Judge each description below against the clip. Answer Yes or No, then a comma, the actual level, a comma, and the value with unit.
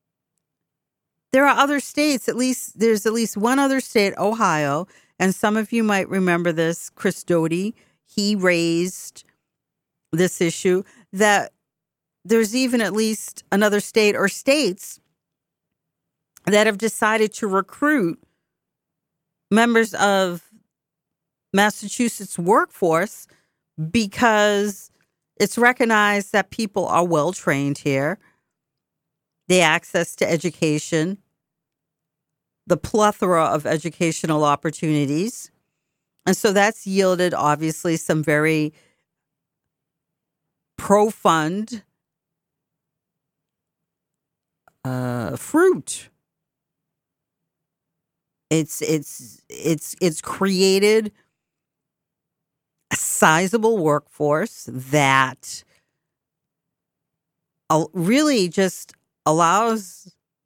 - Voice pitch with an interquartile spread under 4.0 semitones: No, average, 4.9 semitones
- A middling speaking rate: No, slow, 80 wpm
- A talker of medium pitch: Yes, medium, 180 Hz